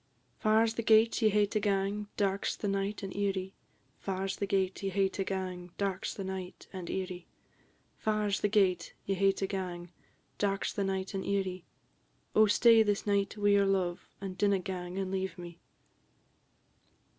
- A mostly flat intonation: Yes, narrow, 1.4 semitones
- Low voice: No, high, 195 Hz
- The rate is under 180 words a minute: No, average, 190 wpm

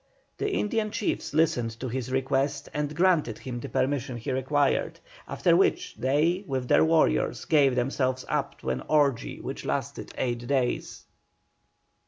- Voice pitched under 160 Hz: Yes, low, 135 Hz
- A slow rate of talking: No, average, 150 wpm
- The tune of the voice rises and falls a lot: No, average, 3.1 semitones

